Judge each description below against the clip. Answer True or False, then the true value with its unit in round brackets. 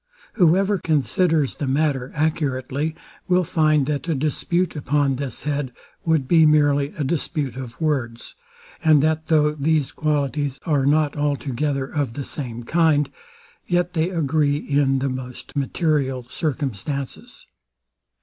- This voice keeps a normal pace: False (130 wpm)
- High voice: False (145 Hz)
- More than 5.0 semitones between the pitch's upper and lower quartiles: False (2.6 semitones)